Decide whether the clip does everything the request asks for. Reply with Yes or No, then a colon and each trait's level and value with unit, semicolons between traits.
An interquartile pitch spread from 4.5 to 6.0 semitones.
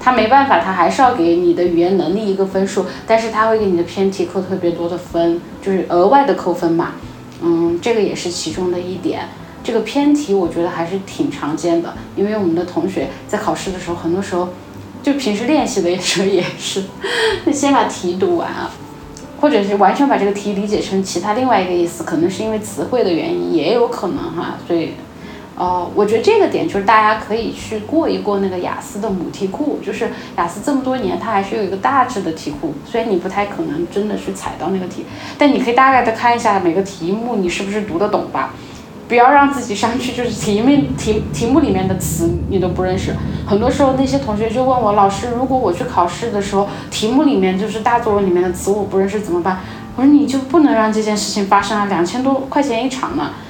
Yes: wide, 5.5 semitones